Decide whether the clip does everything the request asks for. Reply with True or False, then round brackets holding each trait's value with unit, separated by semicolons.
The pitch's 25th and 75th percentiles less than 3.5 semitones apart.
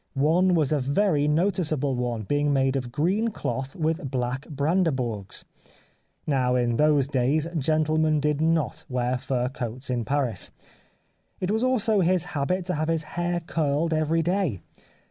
False (4.2 semitones)